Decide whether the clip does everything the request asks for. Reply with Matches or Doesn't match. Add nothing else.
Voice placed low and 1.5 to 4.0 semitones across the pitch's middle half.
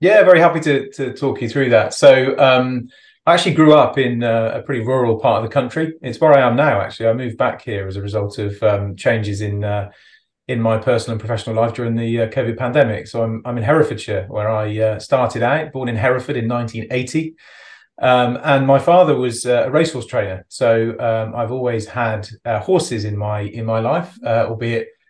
Matches